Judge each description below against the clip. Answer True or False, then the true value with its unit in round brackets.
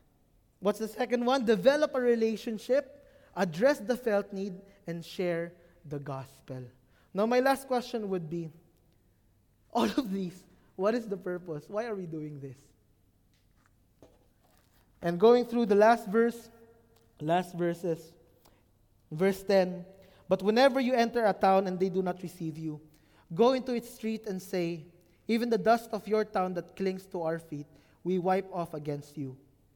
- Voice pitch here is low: False (185 Hz)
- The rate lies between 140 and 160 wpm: True (155 wpm)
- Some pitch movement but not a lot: False (6.4 semitones)